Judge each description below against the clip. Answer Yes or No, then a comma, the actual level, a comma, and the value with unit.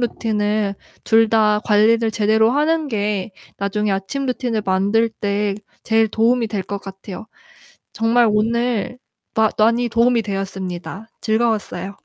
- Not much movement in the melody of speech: Yes, narrow, 2.3 semitones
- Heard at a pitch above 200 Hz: Yes, high, 220 Hz